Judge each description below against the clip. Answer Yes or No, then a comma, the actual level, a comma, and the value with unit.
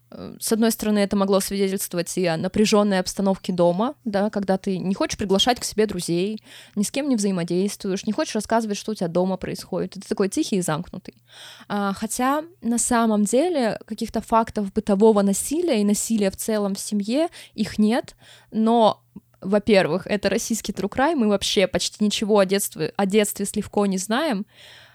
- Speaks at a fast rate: Yes, fast, 170 wpm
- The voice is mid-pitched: No, high, 205 Hz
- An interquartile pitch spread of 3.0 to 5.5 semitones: No, narrow, 2.6 semitones